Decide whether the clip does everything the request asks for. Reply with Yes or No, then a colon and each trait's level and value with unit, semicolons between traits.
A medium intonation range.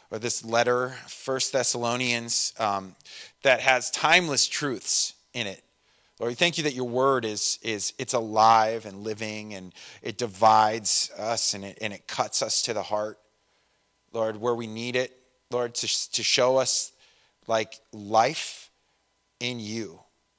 No: narrow, 2.3 semitones